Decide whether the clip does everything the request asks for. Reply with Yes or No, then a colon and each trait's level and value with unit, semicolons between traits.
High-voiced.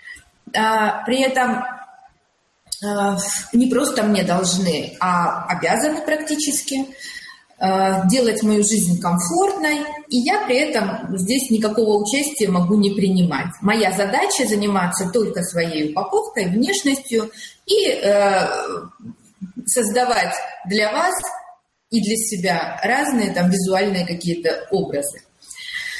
Yes: high, 220 Hz